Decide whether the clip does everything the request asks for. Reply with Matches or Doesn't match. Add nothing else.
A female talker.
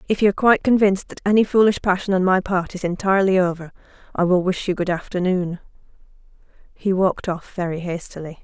Matches